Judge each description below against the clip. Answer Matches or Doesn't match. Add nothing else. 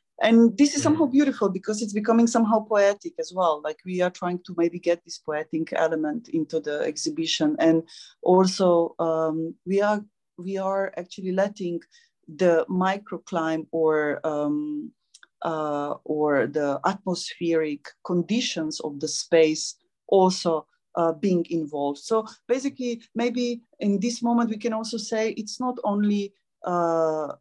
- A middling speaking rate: Matches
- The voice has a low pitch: Doesn't match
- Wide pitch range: Matches